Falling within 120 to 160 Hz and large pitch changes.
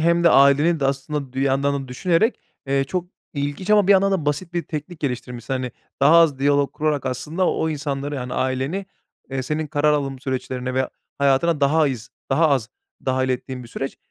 No: medium, 140 Hz; average, 3.2 semitones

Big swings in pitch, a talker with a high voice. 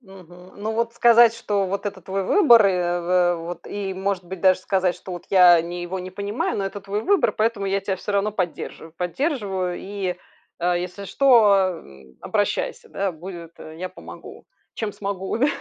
No: narrow, 2.6 semitones; high, 195 Hz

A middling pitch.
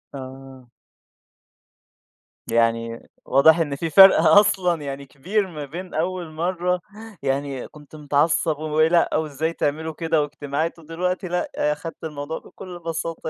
Yes: medium, 160 Hz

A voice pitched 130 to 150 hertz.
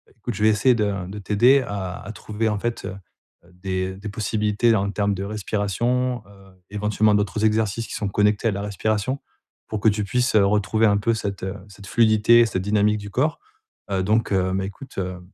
No: low, 105 Hz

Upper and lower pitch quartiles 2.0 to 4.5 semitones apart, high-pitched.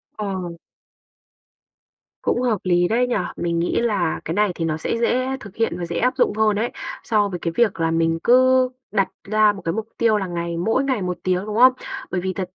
No: average, 4.9 semitones; high, 205 Hz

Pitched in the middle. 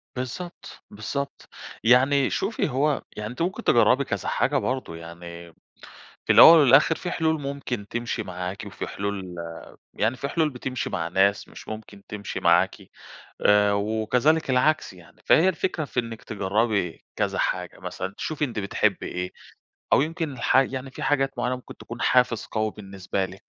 No: low, 120 Hz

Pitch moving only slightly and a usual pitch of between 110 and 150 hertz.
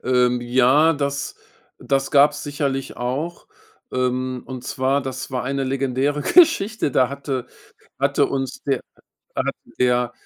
Yes: narrow, 1.9 semitones; low, 135 Hz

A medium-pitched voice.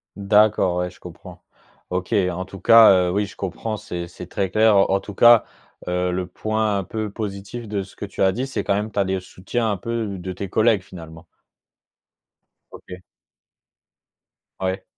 No: low, 100 Hz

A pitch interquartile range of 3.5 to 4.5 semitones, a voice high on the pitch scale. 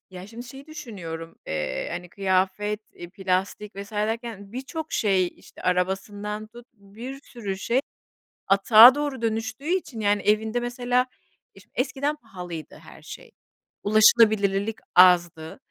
Yes: average, 4.0 semitones; high, 210 Hz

